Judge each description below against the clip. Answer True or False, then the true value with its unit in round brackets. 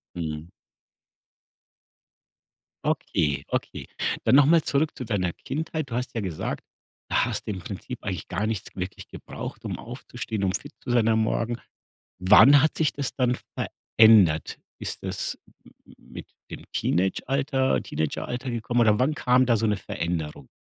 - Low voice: True (115 Hz)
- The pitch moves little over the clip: False (6.0 semitones)